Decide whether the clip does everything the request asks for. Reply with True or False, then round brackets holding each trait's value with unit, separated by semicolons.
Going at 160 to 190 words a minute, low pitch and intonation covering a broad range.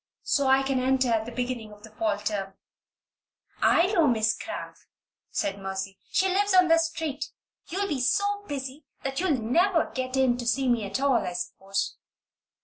False (185 wpm; 260 Hz; 6.6 semitones)